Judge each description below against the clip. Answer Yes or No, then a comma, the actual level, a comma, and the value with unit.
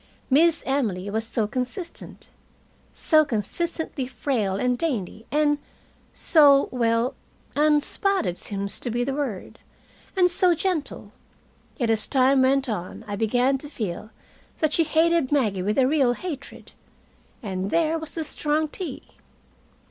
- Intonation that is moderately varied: No, wide, 5.7 semitones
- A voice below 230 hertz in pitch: No, very high, 270 Hz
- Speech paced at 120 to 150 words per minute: Yes, slow, 135 wpm